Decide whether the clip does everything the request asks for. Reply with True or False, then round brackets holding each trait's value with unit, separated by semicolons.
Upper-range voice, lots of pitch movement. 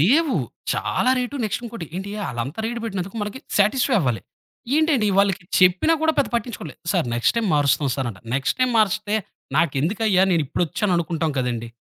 True (195 Hz; 7.6 semitones)